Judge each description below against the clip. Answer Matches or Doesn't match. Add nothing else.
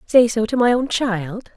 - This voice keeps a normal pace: Doesn't match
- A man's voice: Doesn't match